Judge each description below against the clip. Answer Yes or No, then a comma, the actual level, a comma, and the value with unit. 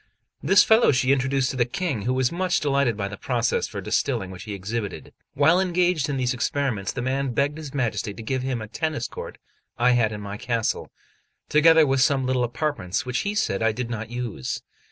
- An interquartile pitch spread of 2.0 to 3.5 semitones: No, average, 4.0 semitones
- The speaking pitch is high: No, low, 130 Hz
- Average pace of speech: No, fast, 210 wpm